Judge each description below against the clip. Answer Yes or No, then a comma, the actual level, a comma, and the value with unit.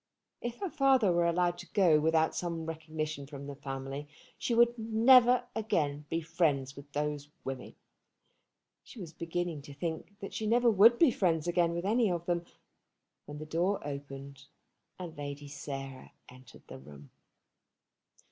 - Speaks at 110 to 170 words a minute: Yes, average, 155 wpm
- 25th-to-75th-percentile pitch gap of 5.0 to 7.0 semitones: Yes, wide, 5.6 semitones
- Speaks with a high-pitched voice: No, medium, 165 Hz